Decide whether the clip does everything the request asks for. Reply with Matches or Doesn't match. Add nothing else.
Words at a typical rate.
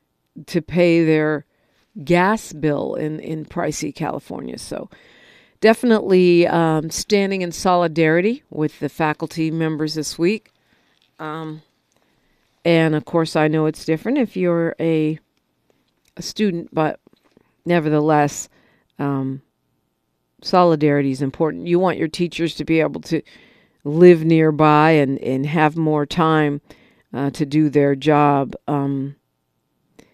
Doesn't match